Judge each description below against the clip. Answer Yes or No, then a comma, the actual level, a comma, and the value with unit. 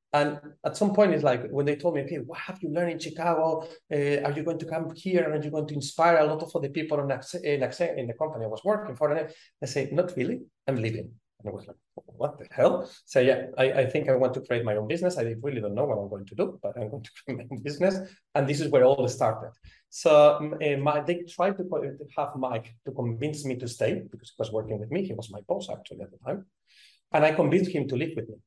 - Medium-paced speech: No, fast, 275 wpm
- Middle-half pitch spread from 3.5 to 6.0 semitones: Yes, average, 4.1 semitones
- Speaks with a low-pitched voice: No, medium, 150 Hz